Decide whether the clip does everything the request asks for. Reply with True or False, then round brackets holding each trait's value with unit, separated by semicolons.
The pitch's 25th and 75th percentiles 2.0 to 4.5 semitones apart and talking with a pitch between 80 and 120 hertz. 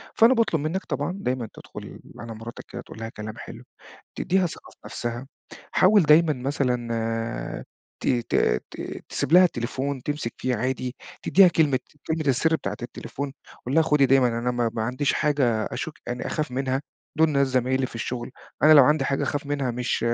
False (4.1 semitones; 130 Hz)